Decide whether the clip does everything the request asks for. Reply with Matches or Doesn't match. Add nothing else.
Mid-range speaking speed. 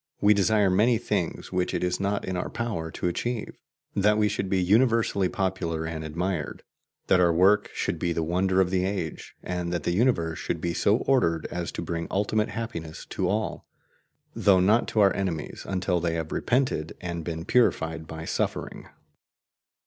Matches